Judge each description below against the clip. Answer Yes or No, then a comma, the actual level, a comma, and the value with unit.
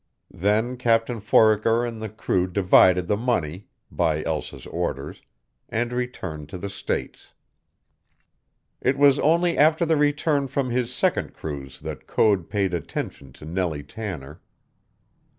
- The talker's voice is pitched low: Yes, low, 105 Hz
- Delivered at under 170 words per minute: Yes, slow, 135 wpm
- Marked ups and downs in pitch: Yes, wide, 6.3 semitones